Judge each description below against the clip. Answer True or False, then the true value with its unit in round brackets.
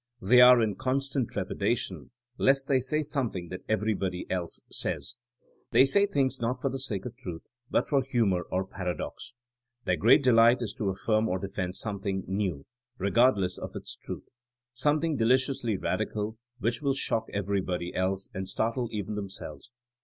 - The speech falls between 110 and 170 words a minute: True (160 wpm)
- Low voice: True (110 Hz)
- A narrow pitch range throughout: False (5.2 semitones)